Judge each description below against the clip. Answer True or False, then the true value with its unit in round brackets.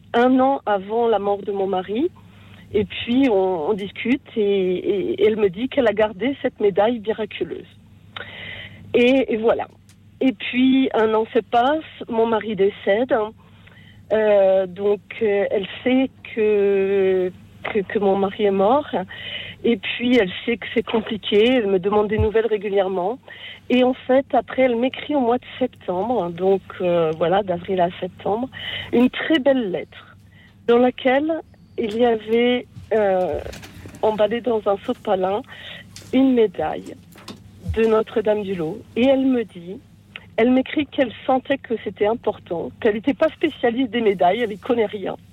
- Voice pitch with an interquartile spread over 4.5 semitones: False (4.0 semitones)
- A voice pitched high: True (220 Hz)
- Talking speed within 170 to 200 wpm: False (160 wpm)